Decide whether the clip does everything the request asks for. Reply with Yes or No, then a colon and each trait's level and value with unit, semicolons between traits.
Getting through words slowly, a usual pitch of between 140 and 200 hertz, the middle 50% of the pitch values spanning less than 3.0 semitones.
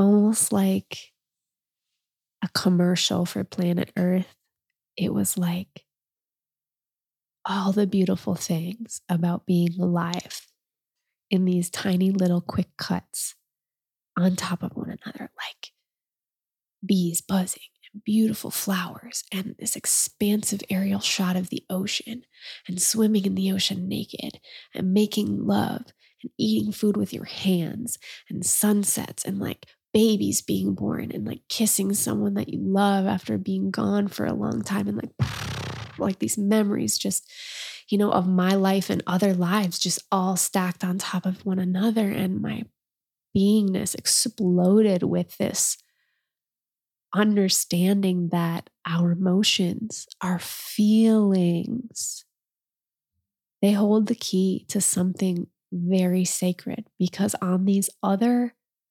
Yes: slow, 125 wpm; high, 190 Hz; narrow, 2.5 semitones